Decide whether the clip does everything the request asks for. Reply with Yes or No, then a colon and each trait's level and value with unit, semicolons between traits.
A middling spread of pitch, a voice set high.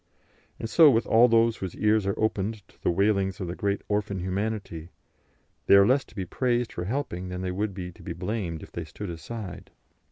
No: average, 3.4 semitones; low, 100 Hz